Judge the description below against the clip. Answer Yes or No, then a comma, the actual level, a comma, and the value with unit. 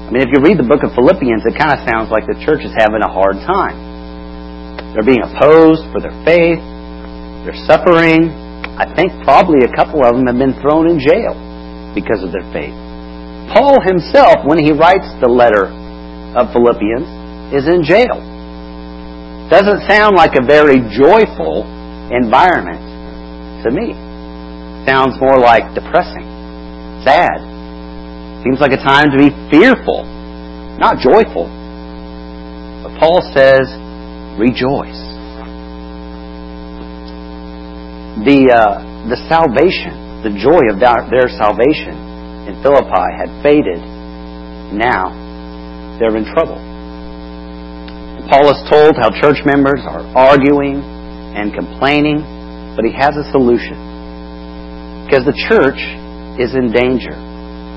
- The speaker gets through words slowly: Yes, slow, 125 wpm